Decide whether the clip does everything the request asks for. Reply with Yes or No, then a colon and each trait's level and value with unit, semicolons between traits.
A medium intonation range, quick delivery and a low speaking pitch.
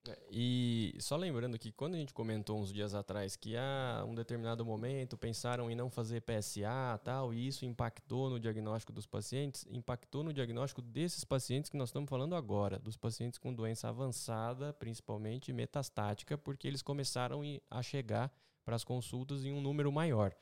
No: average, 3.3 semitones; average, 175 wpm; low, 125 Hz